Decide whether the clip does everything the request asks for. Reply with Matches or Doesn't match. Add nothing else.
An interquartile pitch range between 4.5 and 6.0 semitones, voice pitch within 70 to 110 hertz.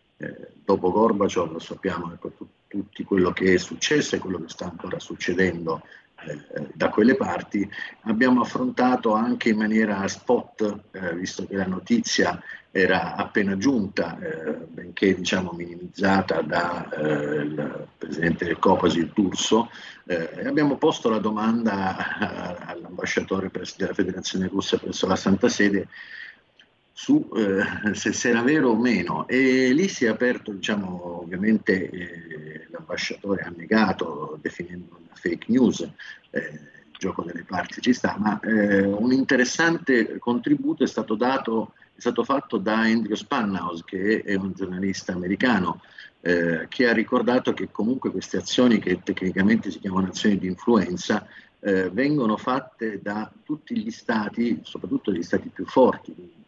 Matches